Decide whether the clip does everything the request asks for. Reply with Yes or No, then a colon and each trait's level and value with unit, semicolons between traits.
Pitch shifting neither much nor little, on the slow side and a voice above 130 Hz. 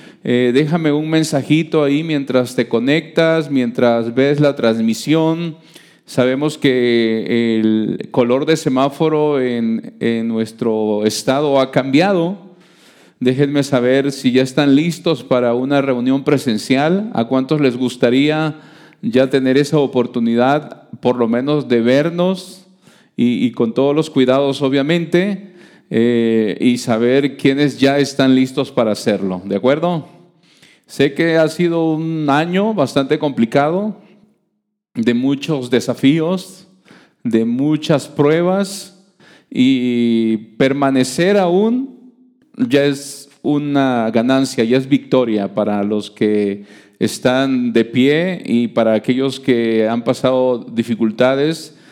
Yes: average, 4.5 semitones; slow, 120 wpm; medium, 140 Hz